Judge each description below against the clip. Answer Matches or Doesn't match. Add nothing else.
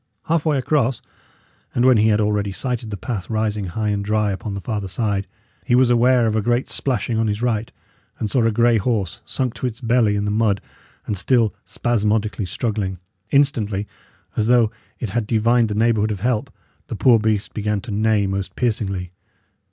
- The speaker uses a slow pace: Doesn't match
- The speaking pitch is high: Doesn't match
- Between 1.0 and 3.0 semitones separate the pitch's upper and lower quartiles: Matches